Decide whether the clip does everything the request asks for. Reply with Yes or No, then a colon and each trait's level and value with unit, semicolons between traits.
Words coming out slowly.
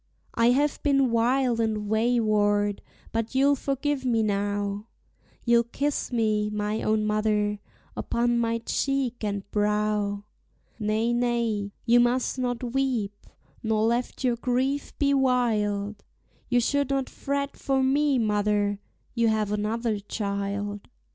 Yes: slow, 130 wpm